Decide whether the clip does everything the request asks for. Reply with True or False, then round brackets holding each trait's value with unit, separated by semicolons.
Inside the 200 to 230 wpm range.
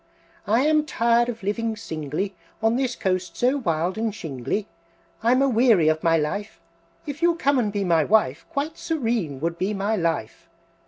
False (175 wpm)